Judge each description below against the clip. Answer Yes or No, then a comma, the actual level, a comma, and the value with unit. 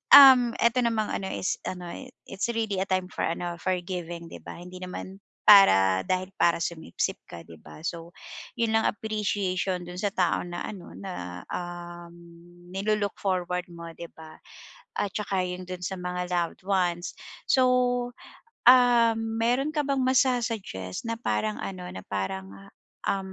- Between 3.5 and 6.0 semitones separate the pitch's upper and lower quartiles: Yes, average, 4.4 semitones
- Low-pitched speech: No, medium, 185 Hz